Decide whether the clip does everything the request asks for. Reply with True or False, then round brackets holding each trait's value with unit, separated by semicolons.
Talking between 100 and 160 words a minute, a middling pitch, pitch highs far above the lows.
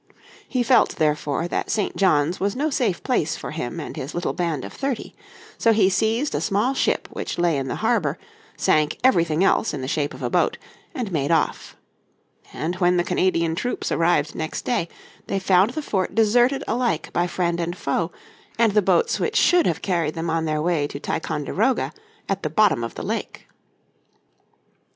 False (190 wpm; 175 Hz; 5.7 semitones)